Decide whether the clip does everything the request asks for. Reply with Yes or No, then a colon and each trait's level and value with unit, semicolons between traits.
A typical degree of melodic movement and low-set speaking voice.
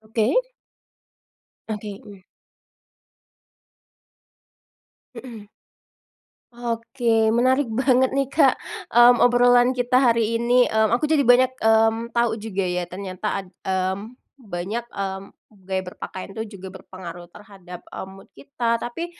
No: average, 4.0 semitones; high, 225 Hz